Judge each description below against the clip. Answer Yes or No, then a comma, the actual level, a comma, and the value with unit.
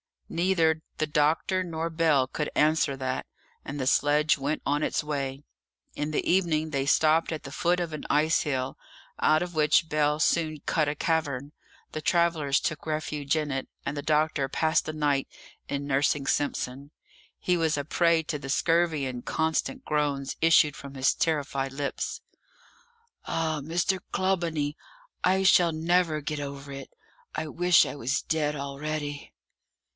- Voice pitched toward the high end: No, medium, 150 Hz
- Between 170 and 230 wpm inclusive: No, average, 160 wpm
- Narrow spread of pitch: Yes, narrow, 2.3 semitones